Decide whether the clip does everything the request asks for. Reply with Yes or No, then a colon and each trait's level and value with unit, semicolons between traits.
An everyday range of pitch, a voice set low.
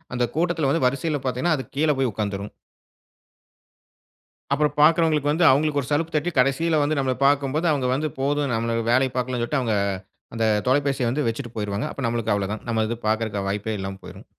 Yes: average, 4.6 semitones; low, 130 Hz